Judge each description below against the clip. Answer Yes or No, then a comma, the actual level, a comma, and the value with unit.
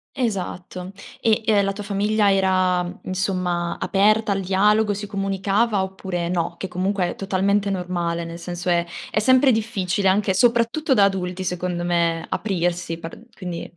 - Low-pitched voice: No, high, 190 Hz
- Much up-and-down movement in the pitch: No, narrow, 2.6 semitones